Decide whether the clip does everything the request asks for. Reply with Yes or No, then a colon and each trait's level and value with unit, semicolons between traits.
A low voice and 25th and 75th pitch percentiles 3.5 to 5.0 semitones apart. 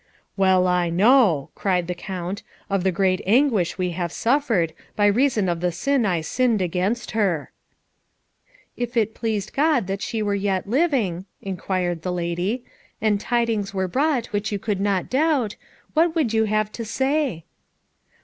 No: high, 205 Hz; average, 4.7 semitones